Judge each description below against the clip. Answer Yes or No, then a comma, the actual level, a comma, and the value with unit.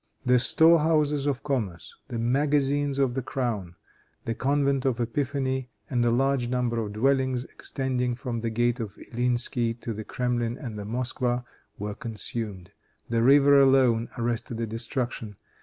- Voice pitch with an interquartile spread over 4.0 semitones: No, average, 2.8 semitones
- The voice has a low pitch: Yes, low, 125 Hz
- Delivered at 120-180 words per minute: Yes, average, 155 wpm